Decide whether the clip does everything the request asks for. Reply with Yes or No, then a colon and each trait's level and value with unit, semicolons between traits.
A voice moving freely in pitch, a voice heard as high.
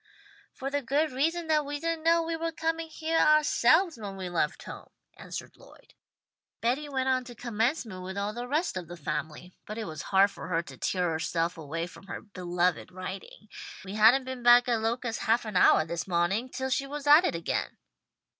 Yes: wide, 8.0 semitones; high, 235 Hz